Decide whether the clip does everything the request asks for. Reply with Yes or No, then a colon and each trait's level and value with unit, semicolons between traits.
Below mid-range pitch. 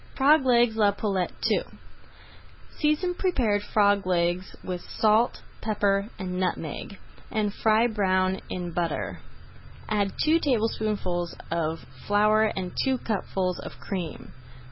No: high, 205 Hz